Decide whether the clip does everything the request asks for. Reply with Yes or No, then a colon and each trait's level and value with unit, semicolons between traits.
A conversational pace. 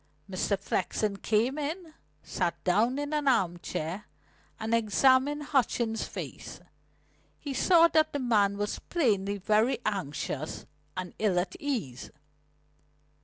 No: slow, 120 wpm